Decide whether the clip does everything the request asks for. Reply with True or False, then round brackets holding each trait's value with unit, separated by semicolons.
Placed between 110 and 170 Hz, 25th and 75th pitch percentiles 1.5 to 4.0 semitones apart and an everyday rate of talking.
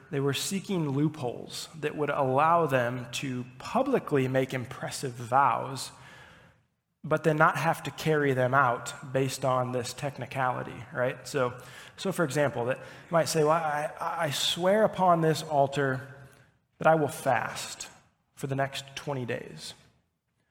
True (140 Hz; 3.2 semitones; 145 wpm)